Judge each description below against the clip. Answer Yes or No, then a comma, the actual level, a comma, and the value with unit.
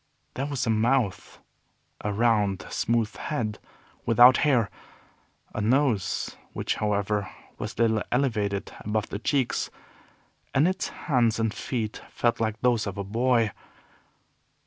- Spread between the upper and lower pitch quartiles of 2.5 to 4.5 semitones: Yes, average, 2.9 semitones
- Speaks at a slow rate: Yes, slow, 125 wpm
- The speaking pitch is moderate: No, low, 115 Hz